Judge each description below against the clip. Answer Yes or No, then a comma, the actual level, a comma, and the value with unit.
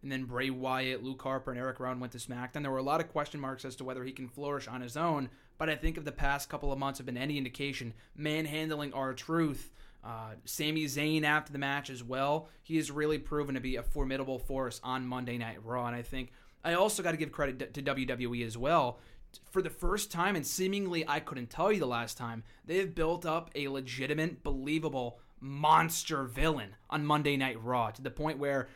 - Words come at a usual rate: No, fast, 230 wpm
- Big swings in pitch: No, average, 3.3 semitones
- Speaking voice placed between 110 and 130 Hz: No, medium, 140 Hz